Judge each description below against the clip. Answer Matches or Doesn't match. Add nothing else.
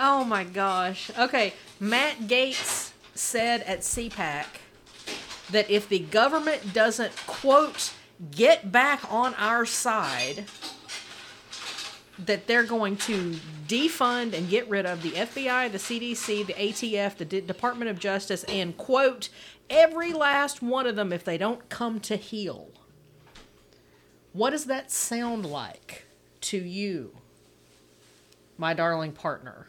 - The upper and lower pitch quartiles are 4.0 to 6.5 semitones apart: Matches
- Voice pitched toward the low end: Doesn't match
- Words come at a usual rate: Doesn't match